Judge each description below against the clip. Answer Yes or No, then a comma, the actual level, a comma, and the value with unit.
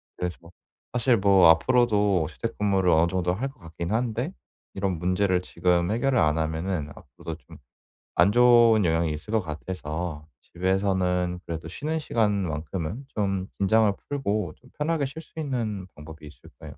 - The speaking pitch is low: Yes, very low, 95 Hz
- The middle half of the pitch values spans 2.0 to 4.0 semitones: No, average, 5.2 semitones